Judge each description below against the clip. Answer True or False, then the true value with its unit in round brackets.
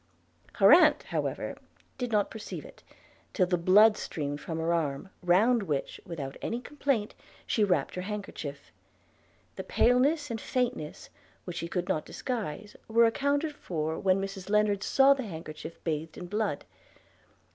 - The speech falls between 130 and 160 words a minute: True (150 wpm)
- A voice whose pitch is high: True (195 Hz)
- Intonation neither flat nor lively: False (5.8 semitones)